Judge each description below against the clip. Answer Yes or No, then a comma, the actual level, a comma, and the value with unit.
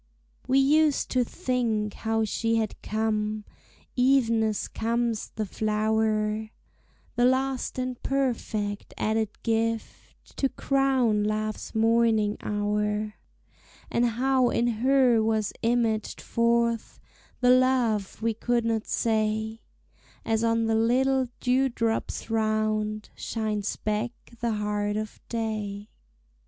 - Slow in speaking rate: Yes, slow, 110 wpm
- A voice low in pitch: No, high, 225 Hz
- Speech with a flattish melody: Yes, narrow, 2.2 semitones